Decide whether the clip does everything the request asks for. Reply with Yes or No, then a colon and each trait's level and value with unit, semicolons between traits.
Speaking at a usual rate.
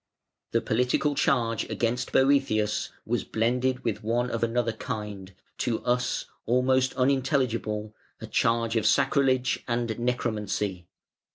No: slow, 115 wpm